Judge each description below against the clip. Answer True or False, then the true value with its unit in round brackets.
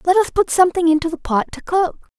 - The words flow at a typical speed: False (245 wpm)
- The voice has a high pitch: True (340 Hz)